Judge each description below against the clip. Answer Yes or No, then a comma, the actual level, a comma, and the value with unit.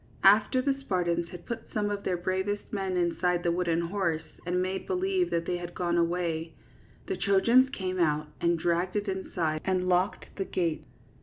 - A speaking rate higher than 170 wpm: Yes, average, 180 wpm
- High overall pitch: No, medium, 180 Hz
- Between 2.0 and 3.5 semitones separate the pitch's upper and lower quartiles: Yes, average, 2.7 semitones